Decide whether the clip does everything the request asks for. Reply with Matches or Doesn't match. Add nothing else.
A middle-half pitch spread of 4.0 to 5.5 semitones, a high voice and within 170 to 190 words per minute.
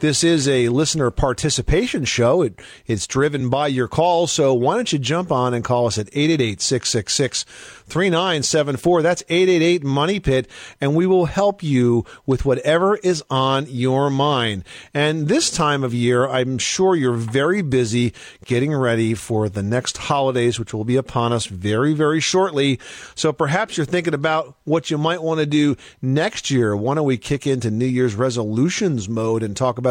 Doesn't match